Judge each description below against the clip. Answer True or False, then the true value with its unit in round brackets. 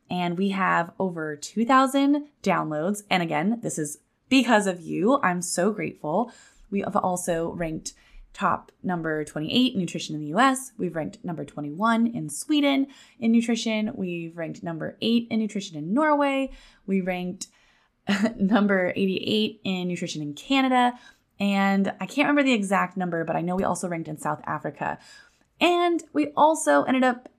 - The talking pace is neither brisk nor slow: True (160 wpm)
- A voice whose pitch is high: True (200 Hz)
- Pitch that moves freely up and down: True (6.4 semitones)